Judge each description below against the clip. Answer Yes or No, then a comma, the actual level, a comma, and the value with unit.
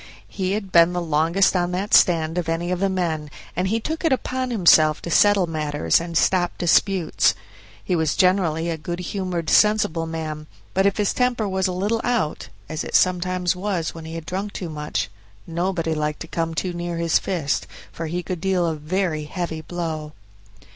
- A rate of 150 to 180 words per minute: No, average, 195 wpm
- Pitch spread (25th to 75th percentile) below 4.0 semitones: Yes, average, 2.9 semitones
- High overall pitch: No, medium, 175 Hz